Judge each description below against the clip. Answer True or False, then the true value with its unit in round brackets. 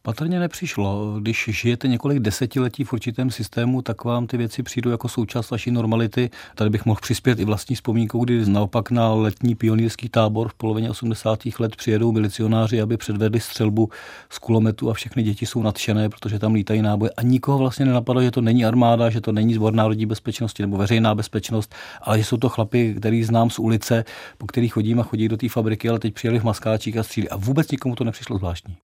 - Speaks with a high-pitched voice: False (115 Hz)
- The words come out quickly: True (205 wpm)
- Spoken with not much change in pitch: True (1.8 semitones)